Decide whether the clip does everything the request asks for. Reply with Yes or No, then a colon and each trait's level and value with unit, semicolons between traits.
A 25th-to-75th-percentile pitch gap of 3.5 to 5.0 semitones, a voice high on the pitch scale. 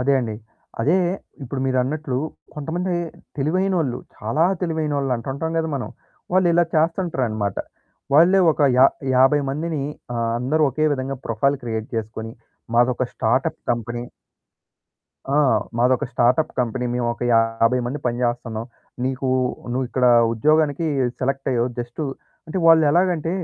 No: average, 4.6 semitones; low, 130 Hz